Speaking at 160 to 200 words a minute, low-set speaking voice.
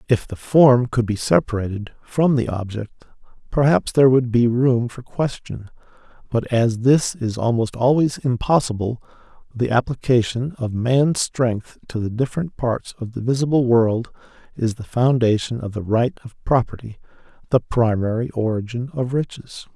No: average, 150 wpm; low, 120 Hz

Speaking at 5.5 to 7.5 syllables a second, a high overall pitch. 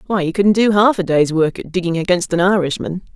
No: 5.8 syllables/s; medium, 180 Hz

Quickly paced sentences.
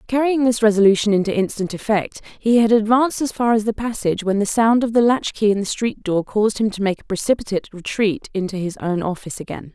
Yes: fast, 230 wpm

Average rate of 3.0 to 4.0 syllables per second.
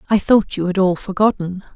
No: 5.5 syllables/s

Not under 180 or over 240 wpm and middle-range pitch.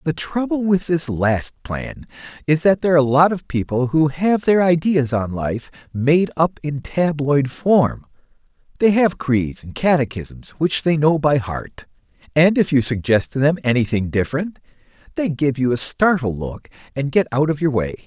Yes: average, 185 wpm; medium, 150 Hz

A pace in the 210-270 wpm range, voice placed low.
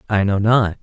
Yes: fast, 220 wpm; low, 105 Hz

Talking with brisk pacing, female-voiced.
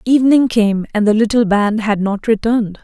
No: average, 190 wpm; female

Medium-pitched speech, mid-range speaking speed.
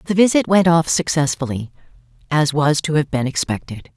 Yes: medium, 155 Hz; average, 165 wpm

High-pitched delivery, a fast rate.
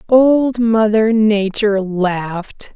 No: high, 215 Hz; slow, 85 wpm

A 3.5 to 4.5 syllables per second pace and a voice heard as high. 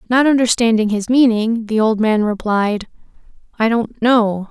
Yes: 4.4 syllables/s; high, 225 Hz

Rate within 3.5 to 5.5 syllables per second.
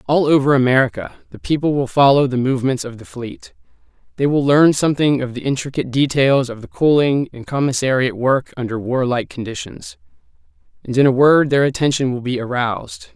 No: 5.8 syllables/s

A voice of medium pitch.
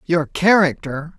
Yes: medium, 165 Hz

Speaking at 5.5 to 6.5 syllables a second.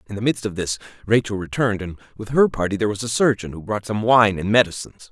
No: 6.7 syllables/s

